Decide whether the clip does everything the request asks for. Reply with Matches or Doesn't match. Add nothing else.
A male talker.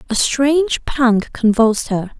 Doesn't match